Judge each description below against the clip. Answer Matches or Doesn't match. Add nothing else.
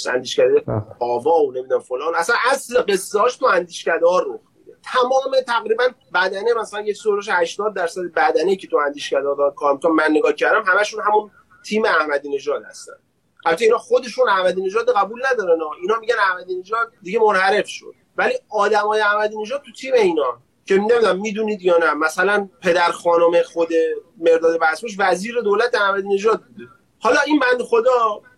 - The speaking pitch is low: Doesn't match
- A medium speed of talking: Doesn't match